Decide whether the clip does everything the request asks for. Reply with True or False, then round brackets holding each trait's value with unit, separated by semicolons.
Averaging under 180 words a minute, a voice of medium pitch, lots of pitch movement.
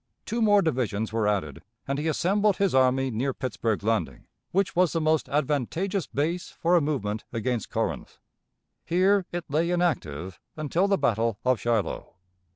True (160 wpm; 145 Hz; 7.5 semitones)